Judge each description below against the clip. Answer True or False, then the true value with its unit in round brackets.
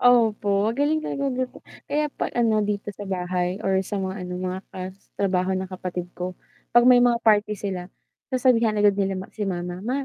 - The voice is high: True (205 Hz)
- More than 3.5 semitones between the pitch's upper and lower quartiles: True (4.4 semitones)